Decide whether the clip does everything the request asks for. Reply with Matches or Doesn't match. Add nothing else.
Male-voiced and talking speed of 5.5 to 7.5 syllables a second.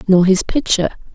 Doesn't match